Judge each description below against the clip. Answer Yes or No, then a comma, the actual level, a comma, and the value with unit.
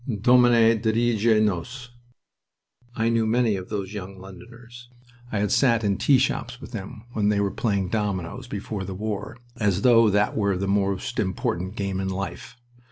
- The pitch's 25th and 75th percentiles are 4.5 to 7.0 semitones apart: No, average, 3.2 semitones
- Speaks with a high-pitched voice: No, low, 105 Hz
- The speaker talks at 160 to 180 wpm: Yes, average, 165 wpm